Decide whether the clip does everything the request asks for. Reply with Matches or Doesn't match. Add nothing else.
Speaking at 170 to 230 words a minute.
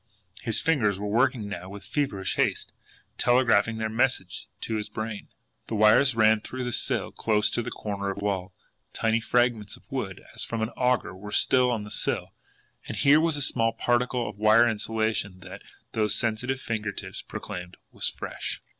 Matches